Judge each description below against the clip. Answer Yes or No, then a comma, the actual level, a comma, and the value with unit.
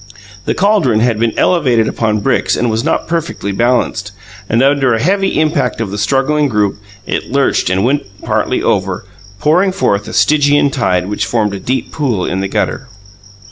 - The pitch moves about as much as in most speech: No, wide, 5.7 semitones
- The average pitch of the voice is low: Yes, low, 120 Hz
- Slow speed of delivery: No, average, 180 wpm